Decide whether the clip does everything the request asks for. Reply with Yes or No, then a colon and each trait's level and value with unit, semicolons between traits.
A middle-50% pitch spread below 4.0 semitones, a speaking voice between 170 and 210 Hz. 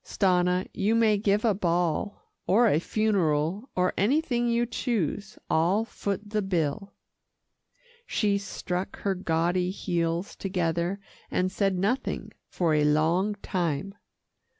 Yes: average, 3.4 semitones; high, 190 Hz